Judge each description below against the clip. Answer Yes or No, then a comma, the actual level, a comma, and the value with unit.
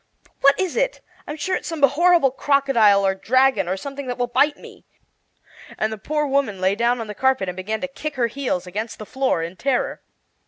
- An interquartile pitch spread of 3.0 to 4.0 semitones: No, average, 5.1 semitones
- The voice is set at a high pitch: Yes, very high, 255 Hz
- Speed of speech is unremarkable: No, fast, 210 wpm